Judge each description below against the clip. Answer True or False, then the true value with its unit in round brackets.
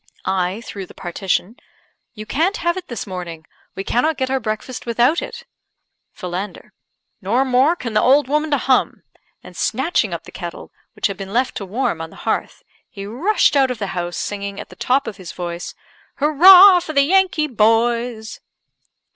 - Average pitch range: False (6.4 semitones)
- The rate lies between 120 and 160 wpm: False (185 wpm)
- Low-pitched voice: False (240 Hz)